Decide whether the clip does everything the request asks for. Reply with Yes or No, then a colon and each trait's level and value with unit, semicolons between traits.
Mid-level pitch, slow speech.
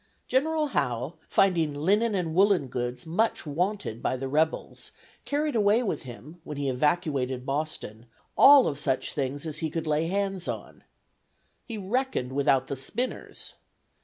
No: medium, 160 Hz; average, 150 wpm